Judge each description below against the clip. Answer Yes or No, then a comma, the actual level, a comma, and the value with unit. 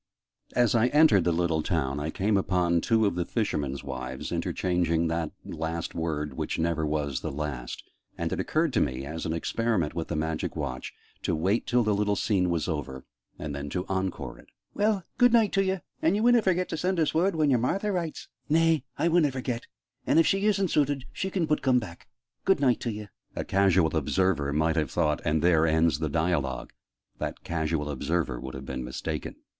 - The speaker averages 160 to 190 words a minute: No, average, 200 wpm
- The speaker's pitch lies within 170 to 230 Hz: No, very low, 90 Hz